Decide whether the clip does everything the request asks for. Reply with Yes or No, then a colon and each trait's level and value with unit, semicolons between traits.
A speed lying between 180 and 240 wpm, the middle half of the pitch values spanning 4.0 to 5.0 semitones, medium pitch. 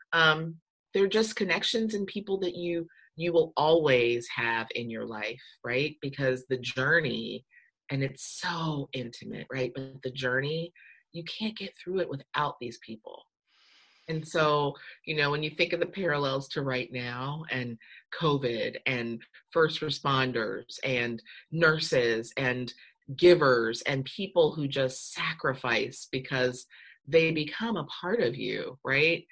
No: average, 145 wpm; average, 4.4 semitones; medium, 145 Hz